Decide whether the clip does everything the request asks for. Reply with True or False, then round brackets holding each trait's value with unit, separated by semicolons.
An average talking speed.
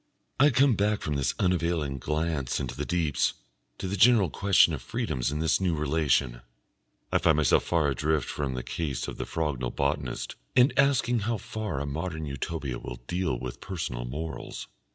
True (175 wpm)